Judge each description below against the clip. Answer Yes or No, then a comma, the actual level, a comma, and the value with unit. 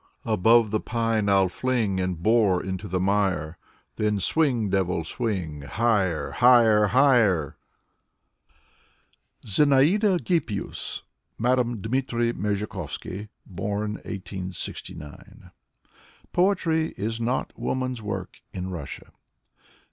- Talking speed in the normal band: No, slow, 95 wpm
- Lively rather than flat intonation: No, average, 4.5 semitones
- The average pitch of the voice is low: Yes, low, 105 Hz